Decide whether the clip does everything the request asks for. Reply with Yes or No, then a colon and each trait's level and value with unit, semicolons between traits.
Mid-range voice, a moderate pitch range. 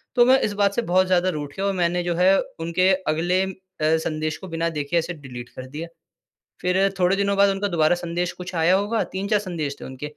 Yes: medium, 175 Hz; average, 3.1 semitones